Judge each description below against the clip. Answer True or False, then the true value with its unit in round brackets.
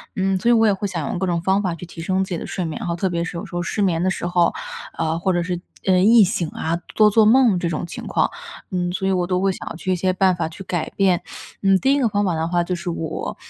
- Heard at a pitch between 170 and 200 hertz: True (185 Hz)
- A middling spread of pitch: False (2.1 semitones)